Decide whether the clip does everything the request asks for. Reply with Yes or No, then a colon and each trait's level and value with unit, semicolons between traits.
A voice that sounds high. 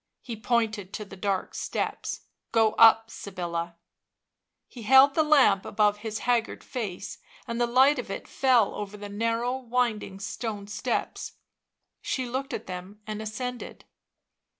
Yes: high, 225 Hz